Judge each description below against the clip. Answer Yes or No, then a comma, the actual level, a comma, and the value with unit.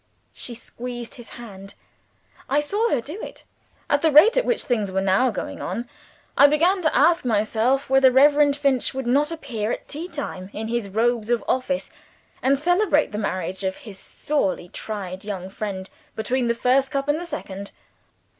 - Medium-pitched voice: No, very high, 250 Hz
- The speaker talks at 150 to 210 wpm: Yes, average, 180 wpm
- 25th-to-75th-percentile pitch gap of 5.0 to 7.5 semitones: Yes, wide, 5.6 semitones